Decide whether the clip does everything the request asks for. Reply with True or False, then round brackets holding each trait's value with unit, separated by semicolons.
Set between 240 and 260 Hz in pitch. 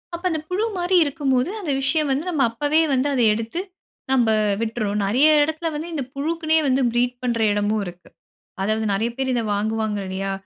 True (255 Hz)